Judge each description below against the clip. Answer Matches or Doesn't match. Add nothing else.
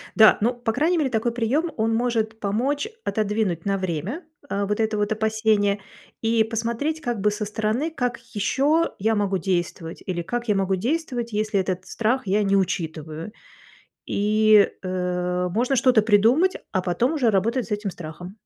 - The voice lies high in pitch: Matches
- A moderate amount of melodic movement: Matches